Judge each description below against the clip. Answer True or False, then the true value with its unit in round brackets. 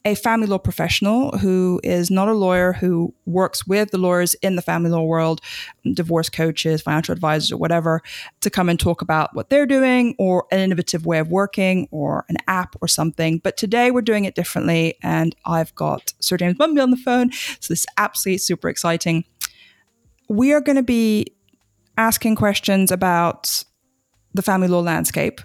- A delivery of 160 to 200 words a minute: True (180 wpm)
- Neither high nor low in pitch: True (180 Hz)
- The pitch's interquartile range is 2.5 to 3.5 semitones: False (4.1 semitones)